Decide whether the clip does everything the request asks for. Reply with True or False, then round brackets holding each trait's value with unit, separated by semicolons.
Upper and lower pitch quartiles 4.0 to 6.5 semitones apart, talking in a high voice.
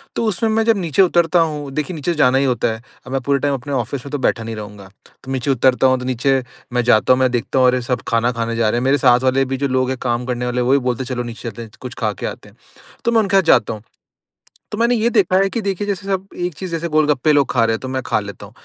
False (5.1 semitones; 130 Hz)